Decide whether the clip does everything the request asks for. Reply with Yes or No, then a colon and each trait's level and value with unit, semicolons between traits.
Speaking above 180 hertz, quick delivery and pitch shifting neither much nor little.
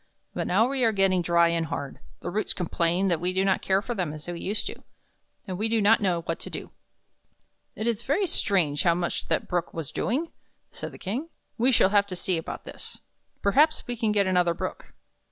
Yes: high, 190 Hz; fast, 220 wpm; average, 4.5 semitones